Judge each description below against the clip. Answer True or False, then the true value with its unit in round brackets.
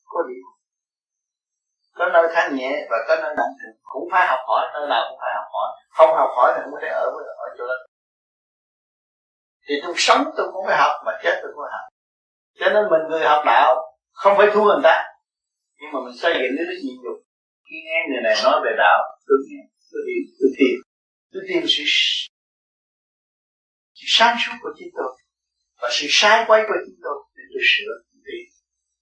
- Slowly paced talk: False (195 wpm)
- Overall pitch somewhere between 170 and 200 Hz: False (270 Hz)